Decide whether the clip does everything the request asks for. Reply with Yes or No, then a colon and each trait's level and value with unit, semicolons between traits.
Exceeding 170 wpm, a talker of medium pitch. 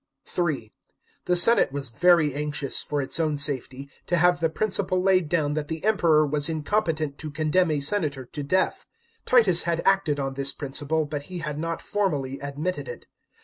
Yes: average, 180 wpm; medium, 155 Hz